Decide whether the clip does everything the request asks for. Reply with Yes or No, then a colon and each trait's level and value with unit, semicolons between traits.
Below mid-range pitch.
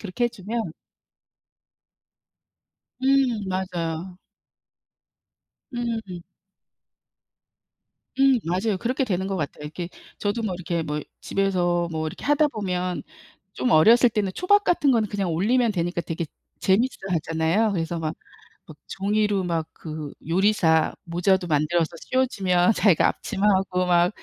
No: high, 190 Hz